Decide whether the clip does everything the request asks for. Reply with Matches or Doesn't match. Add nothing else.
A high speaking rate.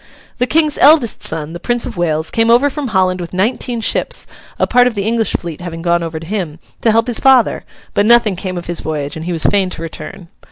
Matches